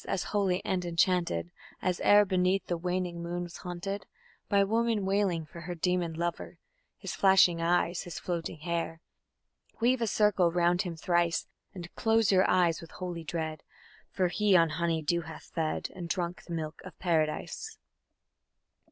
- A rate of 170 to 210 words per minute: No, average, 160 wpm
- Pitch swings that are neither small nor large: No, narrow, 2.0 semitones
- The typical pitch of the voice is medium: Yes, medium, 175 Hz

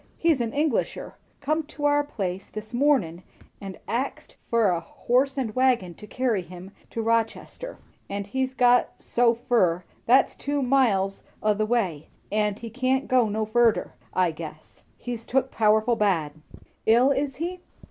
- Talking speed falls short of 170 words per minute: Yes, average, 155 wpm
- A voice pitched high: Yes, high, 230 Hz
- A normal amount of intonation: Yes, average, 4.7 semitones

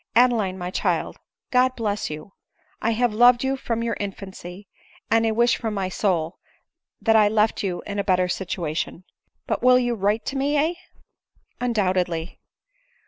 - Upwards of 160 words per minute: Yes, average, 170 wpm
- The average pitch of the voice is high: Yes, high, 210 Hz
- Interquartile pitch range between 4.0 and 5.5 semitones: Yes, average, 4.4 semitones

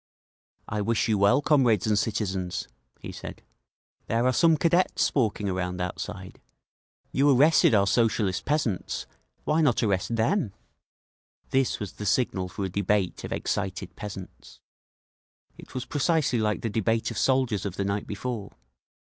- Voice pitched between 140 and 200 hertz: No, low, 105 Hz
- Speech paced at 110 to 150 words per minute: Yes, average, 145 wpm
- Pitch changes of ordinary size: Yes, average, 4.5 semitones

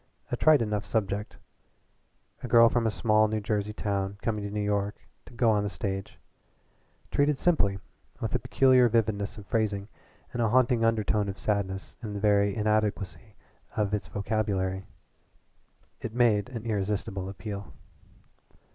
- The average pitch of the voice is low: Yes, low, 105 Hz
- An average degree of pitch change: No, narrow, 2.1 semitones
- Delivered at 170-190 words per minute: No, average, 150 wpm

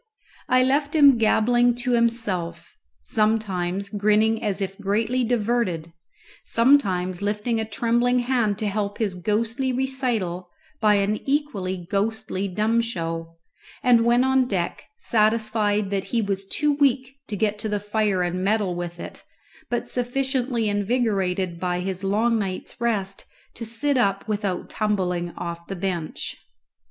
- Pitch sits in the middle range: No, high, 215 Hz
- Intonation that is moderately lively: Yes, average, 3.8 semitones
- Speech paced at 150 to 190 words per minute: No, average, 140 wpm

